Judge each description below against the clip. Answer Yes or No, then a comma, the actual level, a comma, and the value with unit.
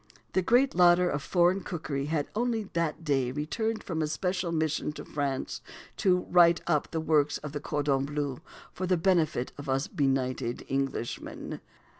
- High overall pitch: No, medium, 155 Hz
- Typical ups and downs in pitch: Yes, average, 4.2 semitones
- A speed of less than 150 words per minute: No, average, 165 wpm